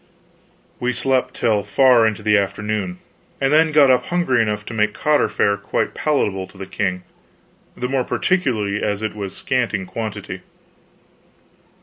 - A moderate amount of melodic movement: Yes, average, 4.2 semitones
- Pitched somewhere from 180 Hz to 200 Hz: No, low, 110 Hz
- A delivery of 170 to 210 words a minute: No, average, 155 wpm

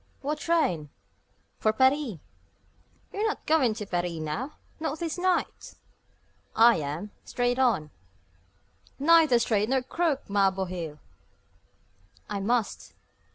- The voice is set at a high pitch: Yes, high, 240 Hz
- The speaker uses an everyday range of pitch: No, wide, 7.7 semitones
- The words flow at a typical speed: No, slow, 110 wpm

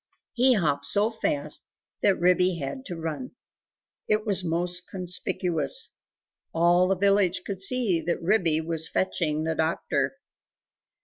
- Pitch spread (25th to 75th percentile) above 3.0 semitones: Yes, average, 3.7 semitones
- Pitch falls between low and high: Yes, medium, 180 Hz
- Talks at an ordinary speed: No, slow, 130 wpm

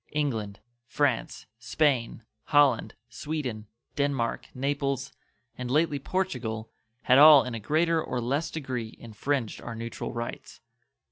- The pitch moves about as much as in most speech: Yes, average, 3.9 semitones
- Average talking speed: No, slow, 120 wpm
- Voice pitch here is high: No, low, 130 Hz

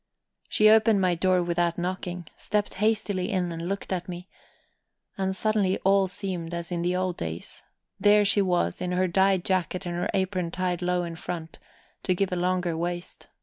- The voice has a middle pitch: Yes, medium, 180 Hz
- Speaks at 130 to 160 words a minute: No, average, 185 wpm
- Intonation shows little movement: Yes, narrow, 1.7 semitones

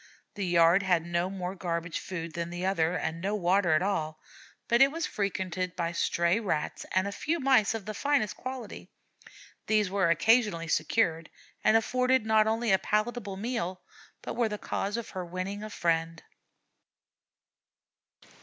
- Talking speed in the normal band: Yes, average, 165 wpm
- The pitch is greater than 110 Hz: Yes, high, 190 Hz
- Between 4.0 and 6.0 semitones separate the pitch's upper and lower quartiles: Yes, average, 4.3 semitones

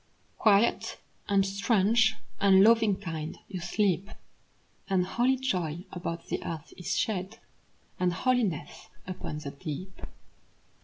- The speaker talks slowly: Yes, slow, 115 wpm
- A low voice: No, high, 190 Hz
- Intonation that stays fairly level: No, average, 3.7 semitones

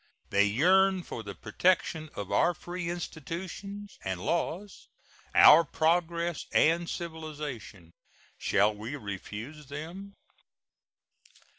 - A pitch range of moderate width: No, wide, 7.3 semitones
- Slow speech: Yes, slow, 100 wpm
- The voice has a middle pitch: Yes, medium, 160 Hz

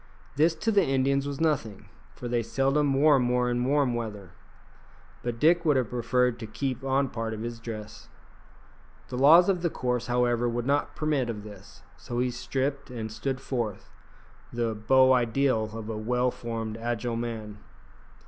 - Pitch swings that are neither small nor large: Yes, average, 3.1 semitones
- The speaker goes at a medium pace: Yes, average, 170 wpm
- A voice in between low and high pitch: No, low, 125 Hz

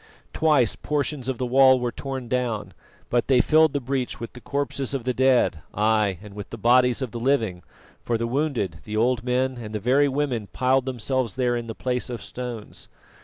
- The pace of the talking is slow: No, fast, 205 wpm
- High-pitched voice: No, low, 125 Hz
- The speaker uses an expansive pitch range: No, narrow, 2.4 semitones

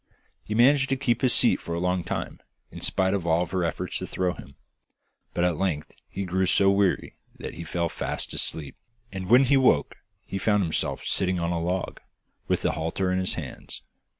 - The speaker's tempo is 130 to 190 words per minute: No, fast, 205 wpm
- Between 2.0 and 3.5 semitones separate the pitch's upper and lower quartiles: Yes, average, 2.8 semitones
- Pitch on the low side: Yes, very low, 95 Hz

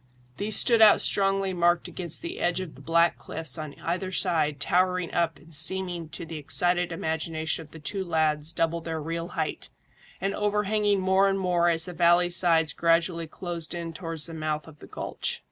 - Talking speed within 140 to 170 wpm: No, average, 190 wpm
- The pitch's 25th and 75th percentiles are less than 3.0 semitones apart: Yes, narrow, 2.4 semitones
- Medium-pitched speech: Yes, medium, 170 Hz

